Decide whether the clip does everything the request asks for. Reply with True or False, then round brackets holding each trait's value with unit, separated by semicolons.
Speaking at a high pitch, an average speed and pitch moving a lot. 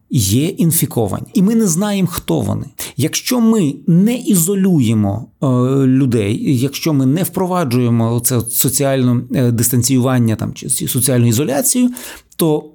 False (135 Hz; 120 wpm; 6.4 semitones)